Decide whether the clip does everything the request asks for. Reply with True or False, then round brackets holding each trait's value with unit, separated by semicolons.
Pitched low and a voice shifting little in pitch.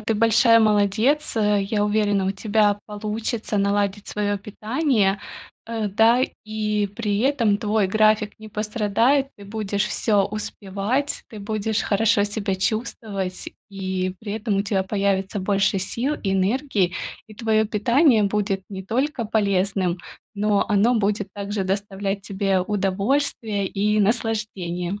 False (210 Hz; 1.8 semitones)